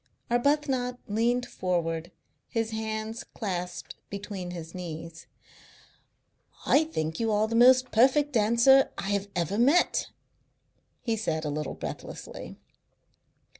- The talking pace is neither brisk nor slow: No, slow, 115 wpm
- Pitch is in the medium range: No, high, 220 Hz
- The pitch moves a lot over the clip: Yes, wide, 5.7 semitones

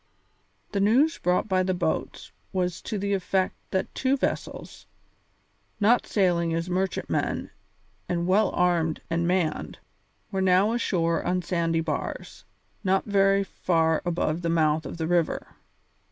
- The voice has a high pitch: No, medium, 180 Hz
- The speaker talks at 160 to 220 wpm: No, average, 140 wpm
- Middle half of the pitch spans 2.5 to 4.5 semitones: Yes, average, 2.8 semitones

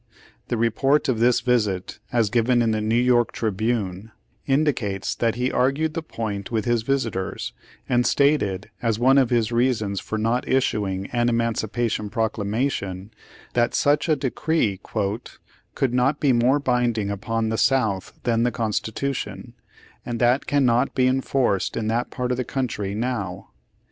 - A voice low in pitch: Yes, low, 120 Hz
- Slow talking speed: No, average, 155 wpm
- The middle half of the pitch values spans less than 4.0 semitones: Yes, average, 3.0 semitones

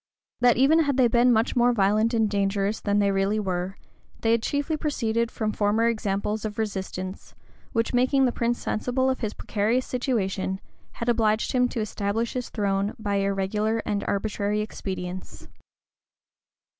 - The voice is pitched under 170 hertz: No, high, 215 Hz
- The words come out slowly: No, average, 155 wpm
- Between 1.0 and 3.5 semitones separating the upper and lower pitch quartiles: Yes, average, 3.1 semitones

